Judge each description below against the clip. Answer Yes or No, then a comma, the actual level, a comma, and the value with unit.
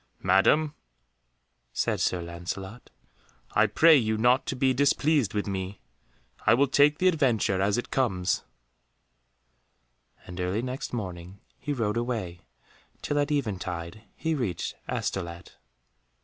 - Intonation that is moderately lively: No, wide, 6.5 semitones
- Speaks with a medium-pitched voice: No, low, 110 Hz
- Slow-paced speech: Yes, slow, 125 wpm